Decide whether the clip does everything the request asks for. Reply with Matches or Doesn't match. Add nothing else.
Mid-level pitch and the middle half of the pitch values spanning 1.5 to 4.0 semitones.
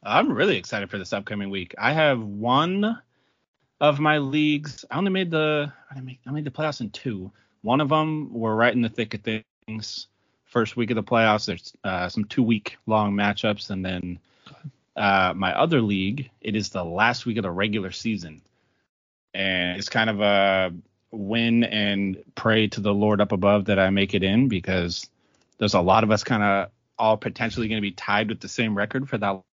Doesn't match